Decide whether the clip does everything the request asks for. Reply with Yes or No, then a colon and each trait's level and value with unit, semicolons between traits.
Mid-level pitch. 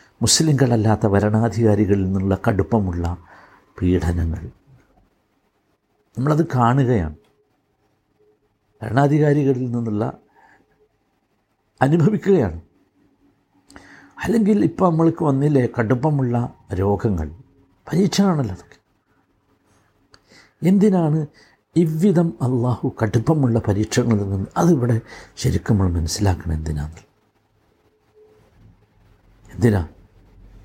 No: low, 110 Hz